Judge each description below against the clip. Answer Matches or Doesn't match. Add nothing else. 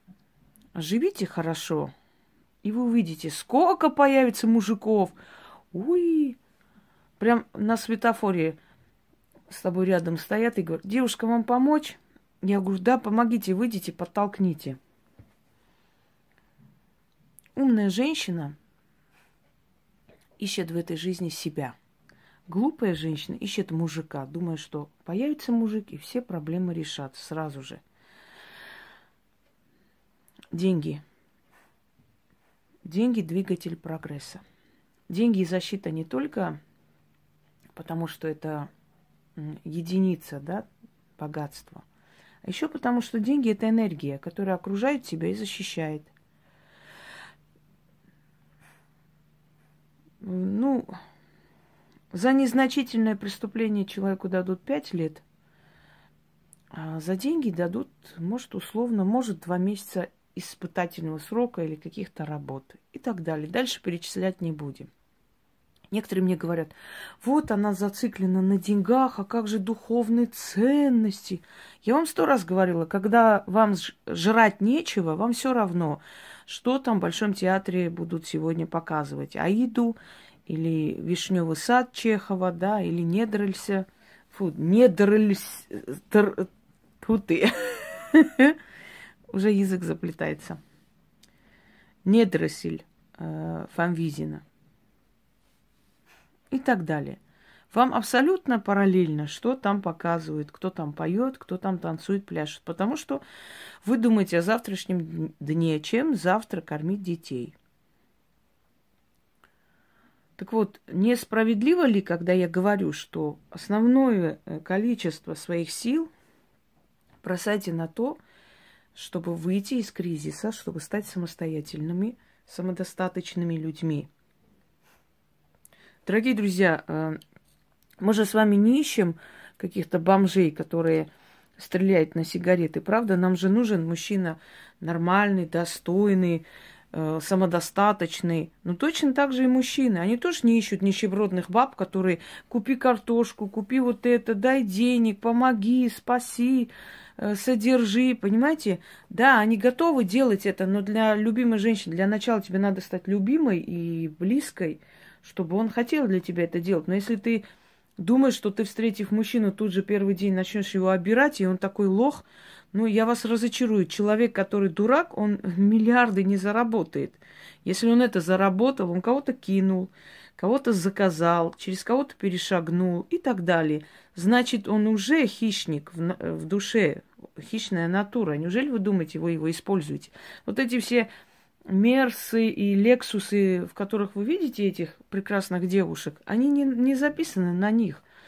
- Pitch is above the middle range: Matches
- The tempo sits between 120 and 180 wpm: Doesn't match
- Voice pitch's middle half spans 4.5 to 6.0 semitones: Matches